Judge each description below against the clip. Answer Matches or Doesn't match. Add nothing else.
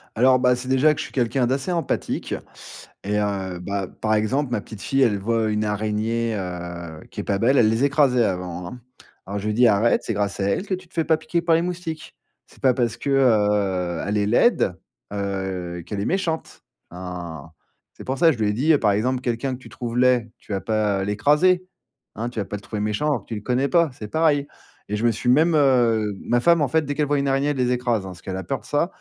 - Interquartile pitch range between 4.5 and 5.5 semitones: Matches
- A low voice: Matches